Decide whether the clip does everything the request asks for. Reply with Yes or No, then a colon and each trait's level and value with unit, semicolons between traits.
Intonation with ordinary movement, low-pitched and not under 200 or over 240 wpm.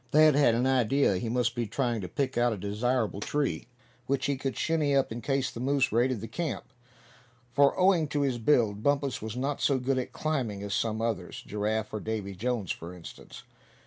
Yes: average, 4.2 semitones; low, 125 Hz; fast, 205 wpm